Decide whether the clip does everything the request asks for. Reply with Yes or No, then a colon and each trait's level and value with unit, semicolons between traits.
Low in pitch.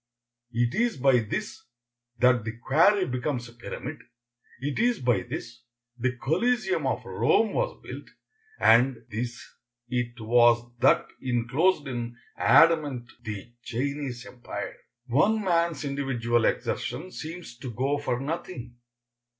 Yes: low, 125 Hz